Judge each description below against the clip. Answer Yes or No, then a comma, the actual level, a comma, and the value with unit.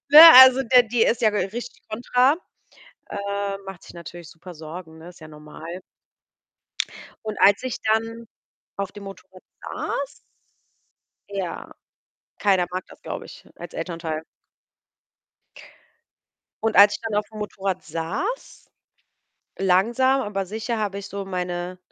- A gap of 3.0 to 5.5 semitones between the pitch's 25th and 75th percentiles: Yes, average, 4.0 semitones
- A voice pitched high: Yes, high, 200 Hz